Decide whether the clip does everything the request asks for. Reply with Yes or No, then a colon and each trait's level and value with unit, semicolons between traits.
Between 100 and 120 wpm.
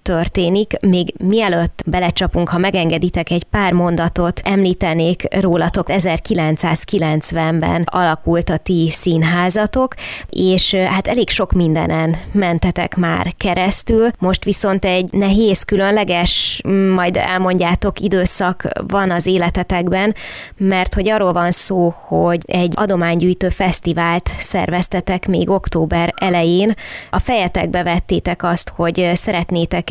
Yes: average, 110 wpm